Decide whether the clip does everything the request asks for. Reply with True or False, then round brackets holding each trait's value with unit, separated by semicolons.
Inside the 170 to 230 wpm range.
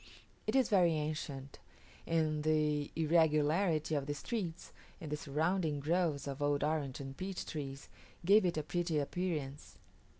False (145 wpm)